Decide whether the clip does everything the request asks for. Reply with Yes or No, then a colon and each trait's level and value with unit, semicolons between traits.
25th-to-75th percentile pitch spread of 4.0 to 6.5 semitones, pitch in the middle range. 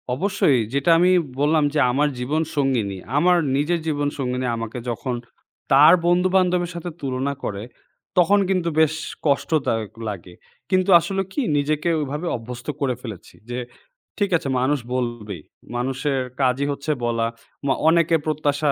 Yes: average, 4.9 semitones; medium, 145 Hz